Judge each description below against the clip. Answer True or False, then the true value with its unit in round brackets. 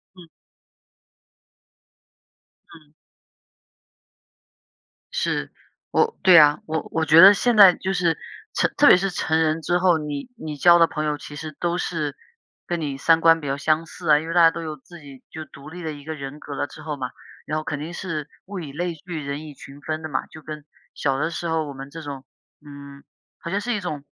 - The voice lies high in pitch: False (155 Hz)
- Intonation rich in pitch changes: False (2.8 semitones)